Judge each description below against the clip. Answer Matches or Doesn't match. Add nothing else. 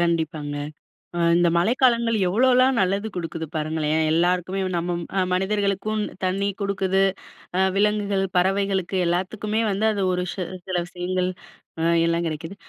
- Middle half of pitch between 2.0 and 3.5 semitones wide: Matches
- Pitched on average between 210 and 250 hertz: Doesn't match